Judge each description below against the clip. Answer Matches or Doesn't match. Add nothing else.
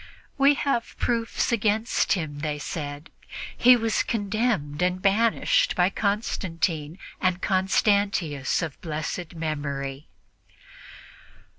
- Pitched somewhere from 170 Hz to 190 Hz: Matches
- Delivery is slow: Matches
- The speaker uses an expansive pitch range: Matches